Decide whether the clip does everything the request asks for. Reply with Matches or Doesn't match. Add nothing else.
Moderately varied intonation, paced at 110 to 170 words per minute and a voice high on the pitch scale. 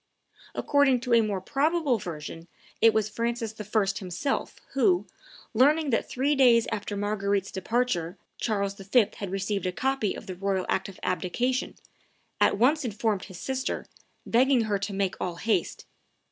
Matches